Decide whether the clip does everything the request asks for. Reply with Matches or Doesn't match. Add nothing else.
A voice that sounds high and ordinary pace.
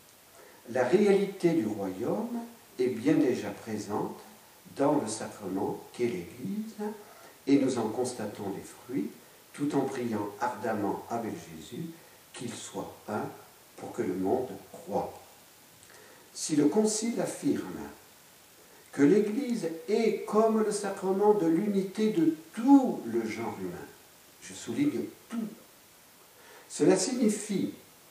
Doesn't match